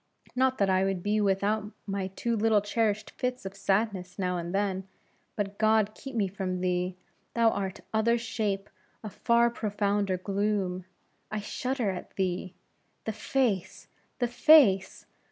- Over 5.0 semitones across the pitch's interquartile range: No, average, 2.7 semitones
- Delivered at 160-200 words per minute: No, average, 145 wpm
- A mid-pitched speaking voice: No, high, 205 Hz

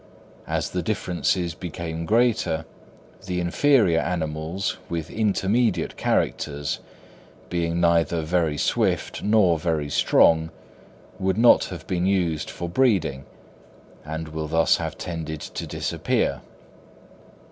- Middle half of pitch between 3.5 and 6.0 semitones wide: No, average, 2.9 semitones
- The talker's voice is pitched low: Yes, very low, 85 Hz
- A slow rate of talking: Yes, slow, 110 wpm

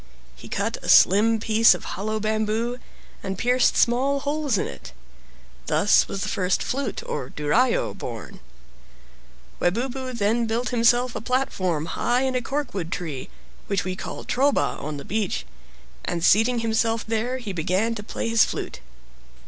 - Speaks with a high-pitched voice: Yes, high, 225 Hz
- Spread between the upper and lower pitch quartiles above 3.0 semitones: Yes, average, 4.3 semitones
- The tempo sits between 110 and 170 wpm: Yes, average, 150 wpm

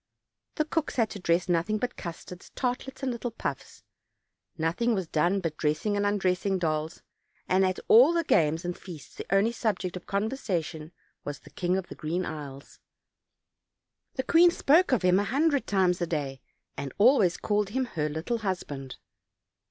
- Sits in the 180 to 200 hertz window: Yes, medium, 185 Hz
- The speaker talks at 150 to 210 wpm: Yes, average, 170 wpm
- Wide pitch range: Yes, wide, 5.9 semitones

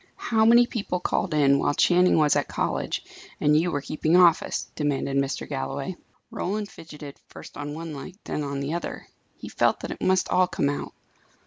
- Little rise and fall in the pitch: No, average, 4.2 semitones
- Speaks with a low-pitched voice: No, medium, 155 Hz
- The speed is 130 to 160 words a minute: No, average, 190 wpm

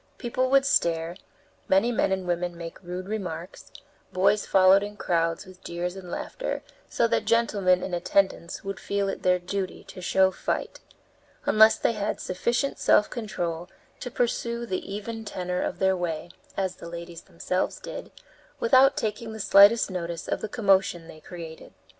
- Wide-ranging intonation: No, average, 3.5 semitones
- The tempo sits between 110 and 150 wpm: No, average, 165 wpm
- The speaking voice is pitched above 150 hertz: Yes, high, 190 Hz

